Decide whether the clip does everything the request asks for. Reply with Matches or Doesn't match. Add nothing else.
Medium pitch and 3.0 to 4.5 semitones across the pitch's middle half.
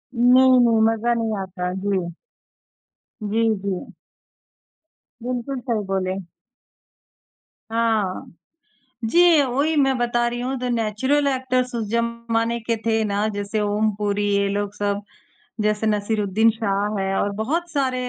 Doesn't match